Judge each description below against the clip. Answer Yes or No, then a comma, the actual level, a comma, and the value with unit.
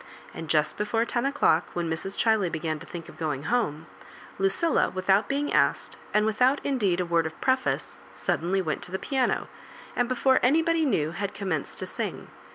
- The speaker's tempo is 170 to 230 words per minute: Yes, average, 180 wpm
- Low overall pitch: No, high, 195 Hz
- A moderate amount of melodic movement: No, wide, 7.3 semitones